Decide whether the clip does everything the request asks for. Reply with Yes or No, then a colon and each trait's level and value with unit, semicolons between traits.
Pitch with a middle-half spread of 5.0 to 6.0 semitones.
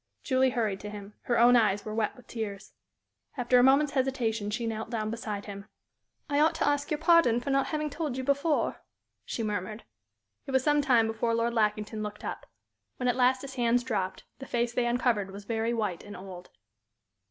No: average, 3.8 semitones